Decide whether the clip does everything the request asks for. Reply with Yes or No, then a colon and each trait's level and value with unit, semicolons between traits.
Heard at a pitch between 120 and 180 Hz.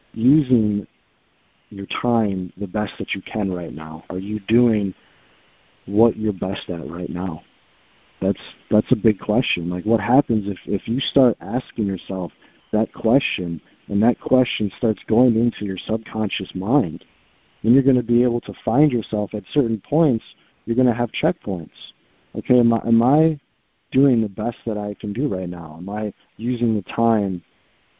No: low, 110 Hz